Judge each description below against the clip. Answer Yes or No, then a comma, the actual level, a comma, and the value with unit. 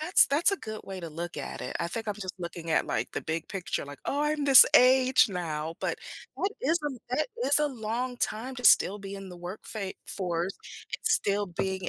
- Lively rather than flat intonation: Yes, wide, 6.4 semitones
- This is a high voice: Yes, high, 205 Hz